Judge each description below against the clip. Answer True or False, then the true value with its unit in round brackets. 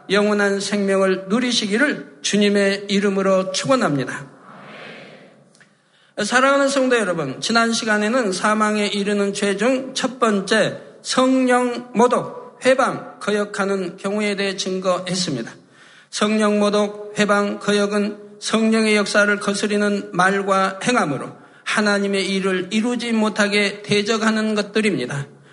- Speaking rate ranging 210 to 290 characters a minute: True (275 characters per minute)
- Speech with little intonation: True (2.1 semitones)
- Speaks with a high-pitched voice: True (205 Hz)